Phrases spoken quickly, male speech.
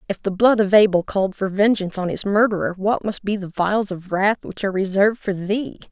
No: fast, 235 wpm; female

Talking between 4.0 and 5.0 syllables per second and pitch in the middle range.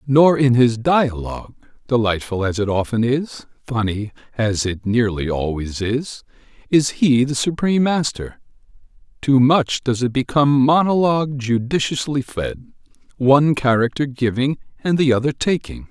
No: 4.6 syllables/s; low, 125 Hz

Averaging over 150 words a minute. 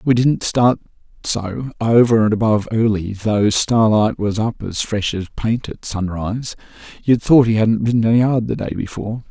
Yes: average, 180 wpm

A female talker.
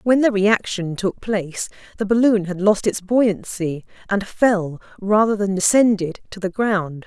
Yes: female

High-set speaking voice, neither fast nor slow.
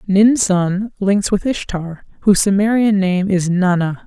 Yes: high, 195 Hz; average, 145 wpm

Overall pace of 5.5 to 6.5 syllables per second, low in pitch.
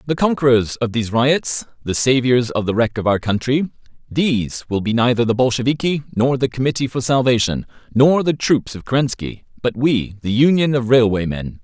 No: 5.3 syllables/s; low, 125 Hz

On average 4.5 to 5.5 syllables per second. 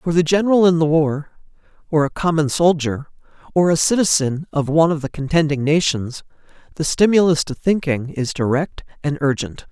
Yes: 5.4 syllables/s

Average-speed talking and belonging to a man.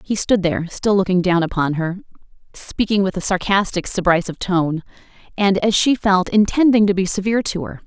No: average, 185 wpm; female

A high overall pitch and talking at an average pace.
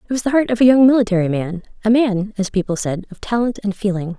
No: high, 210 Hz; fast, 260 wpm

